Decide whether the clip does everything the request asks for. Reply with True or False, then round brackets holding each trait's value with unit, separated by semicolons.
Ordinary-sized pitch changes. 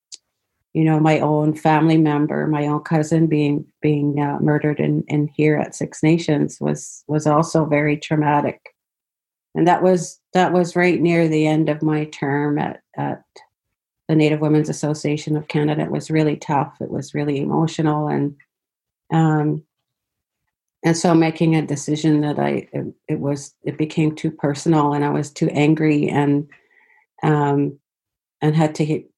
False (1.4 semitones)